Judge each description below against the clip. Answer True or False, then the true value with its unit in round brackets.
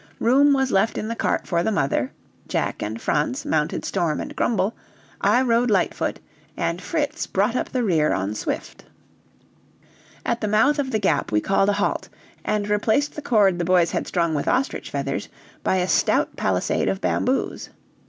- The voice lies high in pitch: True (205 Hz)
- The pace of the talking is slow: False (180 wpm)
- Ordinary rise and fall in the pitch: False (6.1 semitones)